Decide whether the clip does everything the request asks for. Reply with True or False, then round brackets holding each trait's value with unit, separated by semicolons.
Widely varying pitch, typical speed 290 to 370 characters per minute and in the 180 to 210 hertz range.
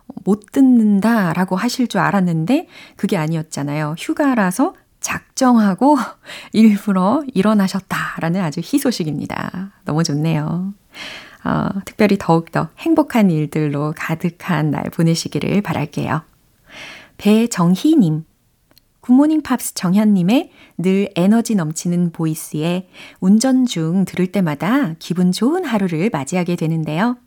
False (5.9 semitones; 275 characters per minute; 190 Hz)